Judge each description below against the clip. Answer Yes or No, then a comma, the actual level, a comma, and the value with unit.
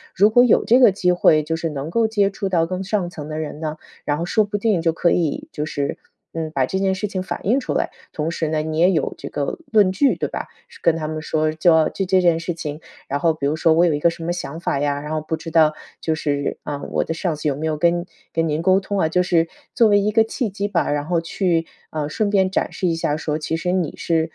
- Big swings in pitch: No, average, 3.4 semitones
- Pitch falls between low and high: Yes, medium, 165 Hz